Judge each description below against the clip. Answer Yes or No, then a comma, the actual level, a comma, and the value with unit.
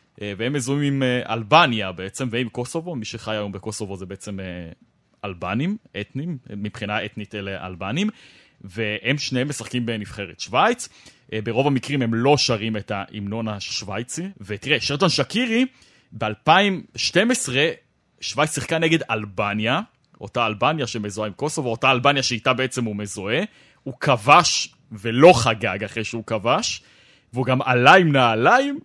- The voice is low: Yes, low, 120 Hz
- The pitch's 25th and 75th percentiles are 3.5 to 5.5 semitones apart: Yes, average, 5.1 semitones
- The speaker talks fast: No, average, 130 wpm